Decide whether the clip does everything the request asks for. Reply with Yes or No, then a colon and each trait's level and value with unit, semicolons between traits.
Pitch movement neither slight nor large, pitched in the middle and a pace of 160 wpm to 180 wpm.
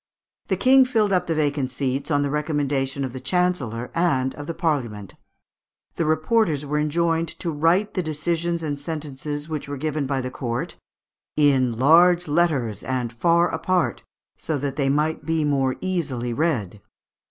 Yes: average, 3.9 semitones; medium, 150 Hz; average, 165 wpm